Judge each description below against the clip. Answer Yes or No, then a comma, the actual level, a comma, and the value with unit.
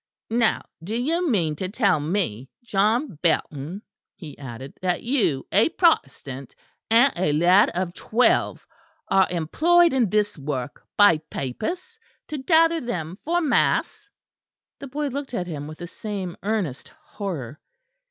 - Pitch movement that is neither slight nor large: No, wide, 8.6 semitones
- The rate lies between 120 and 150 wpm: Yes, average, 140 wpm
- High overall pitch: Yes, high, 195 Hz